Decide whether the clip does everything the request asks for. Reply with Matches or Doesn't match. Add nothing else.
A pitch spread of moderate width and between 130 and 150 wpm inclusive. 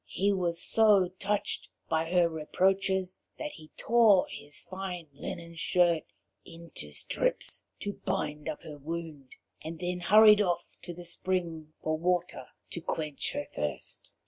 Matches